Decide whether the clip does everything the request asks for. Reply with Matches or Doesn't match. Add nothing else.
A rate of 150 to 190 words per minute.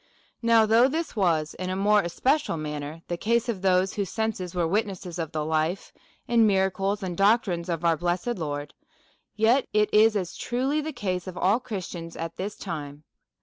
Matches